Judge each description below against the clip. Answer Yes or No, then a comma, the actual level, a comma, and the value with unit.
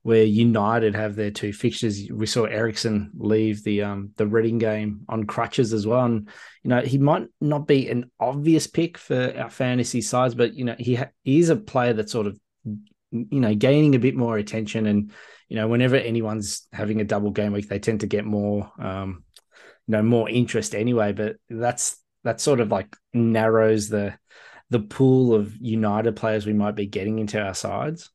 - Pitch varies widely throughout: No, narrow, 2.5 semitones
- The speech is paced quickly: No, average, 195 wpm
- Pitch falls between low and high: No, low, 110 Hz